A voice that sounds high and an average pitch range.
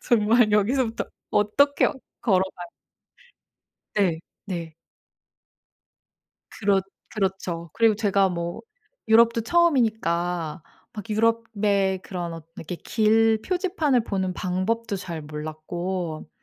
Yes: high, 200 Hz; average, 4.4 semitones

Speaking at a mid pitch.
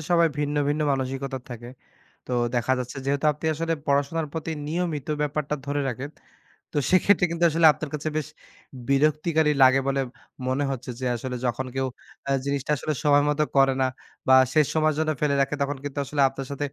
Yes: medium, 145 Hz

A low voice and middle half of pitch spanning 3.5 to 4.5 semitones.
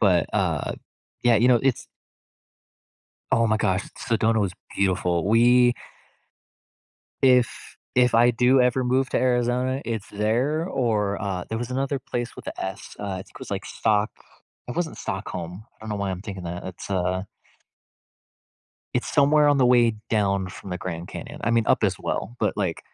Yes: low, 115 Hz; average, 4.2 semitones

